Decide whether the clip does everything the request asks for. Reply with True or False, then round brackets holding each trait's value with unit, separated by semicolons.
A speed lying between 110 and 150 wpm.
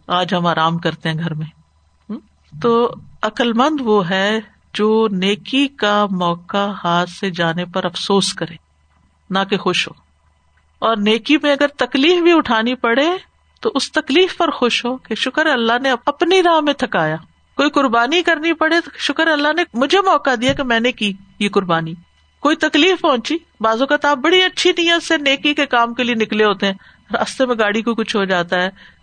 False (185 wpm)